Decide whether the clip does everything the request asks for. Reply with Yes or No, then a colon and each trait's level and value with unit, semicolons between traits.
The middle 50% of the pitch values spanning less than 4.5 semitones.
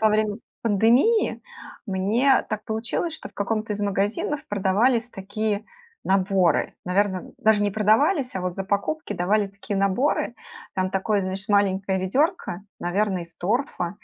Yes: narrow, 2.6 semitones